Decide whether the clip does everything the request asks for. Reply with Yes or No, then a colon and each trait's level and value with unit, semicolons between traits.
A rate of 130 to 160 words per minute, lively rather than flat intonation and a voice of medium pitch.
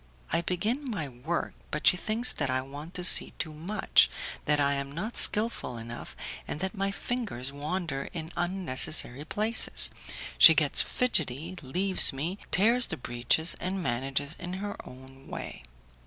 Yes: average, 155 wpm; wide, 5.9 semitones; medium, 165 Hz